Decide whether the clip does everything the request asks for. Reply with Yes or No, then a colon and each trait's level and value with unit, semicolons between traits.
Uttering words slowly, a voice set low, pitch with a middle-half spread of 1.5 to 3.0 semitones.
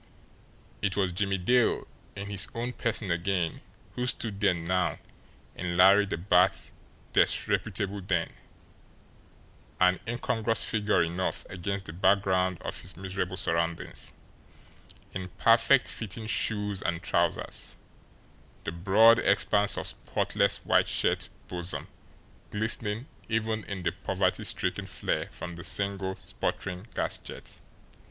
Yes: slow, 120 wpm; very low, 95 Hz; average, 2.7 semitones